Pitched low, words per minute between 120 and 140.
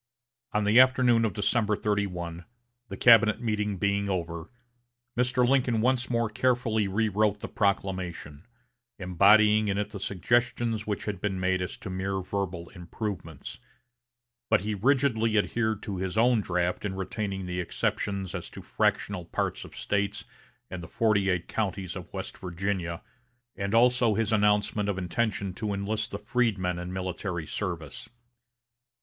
No: low, 100 Hz; average, 150 wpm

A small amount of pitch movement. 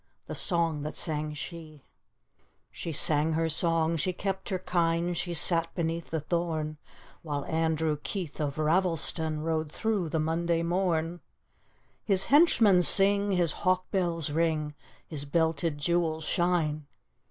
Yes: narrow, 2.1 semitones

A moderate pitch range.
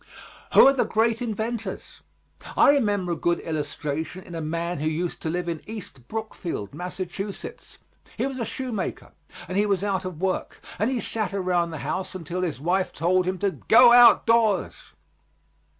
Yes: average, 4.3 semitones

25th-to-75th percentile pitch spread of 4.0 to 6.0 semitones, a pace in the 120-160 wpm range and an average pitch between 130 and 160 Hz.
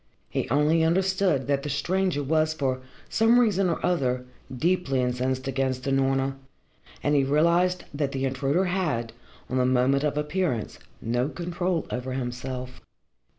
Yes: average, 4.8 semitones; average, 145 wpm; medium, 140 Hz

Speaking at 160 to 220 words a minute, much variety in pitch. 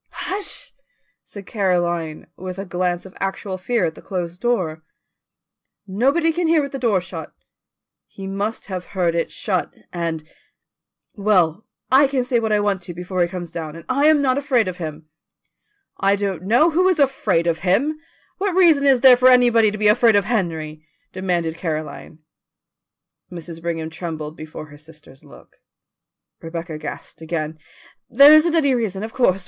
Yes: average, 170 wpm; wide, 6.6 semitones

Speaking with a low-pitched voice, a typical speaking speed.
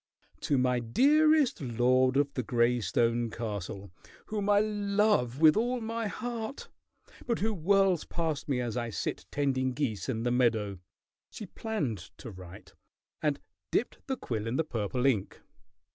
Yes: low, 130 Hz; average, 155 wpm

